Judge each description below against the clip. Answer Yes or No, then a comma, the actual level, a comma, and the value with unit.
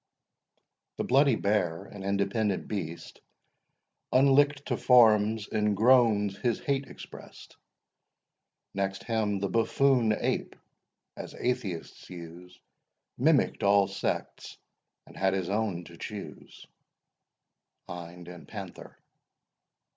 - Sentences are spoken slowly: Yes, slow, 100 wpm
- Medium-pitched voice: No, low, 100 Hz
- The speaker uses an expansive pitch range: No, average, 3.3 semitones